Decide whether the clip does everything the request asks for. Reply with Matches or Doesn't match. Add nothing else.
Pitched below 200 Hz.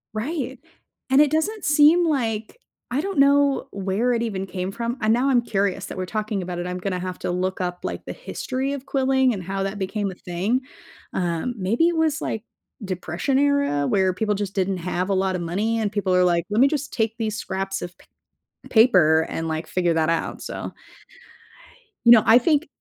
Doesn't match